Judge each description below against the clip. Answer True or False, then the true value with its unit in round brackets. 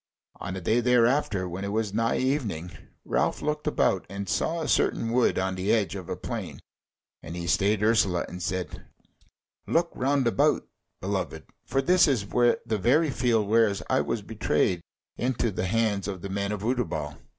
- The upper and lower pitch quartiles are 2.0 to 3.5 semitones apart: False (4.6 semitones)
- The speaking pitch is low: True (105 Hz)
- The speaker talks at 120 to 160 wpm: False (175 wpm)